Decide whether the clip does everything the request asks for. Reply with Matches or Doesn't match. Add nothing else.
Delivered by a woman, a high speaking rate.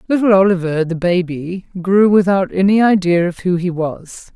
Doesn't match